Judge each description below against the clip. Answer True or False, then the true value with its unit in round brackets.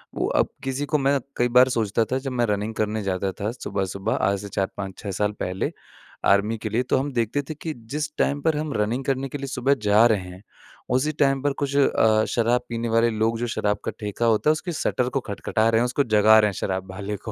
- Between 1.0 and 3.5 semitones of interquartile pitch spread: False (4.6 semitones)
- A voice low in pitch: True (115 Hz)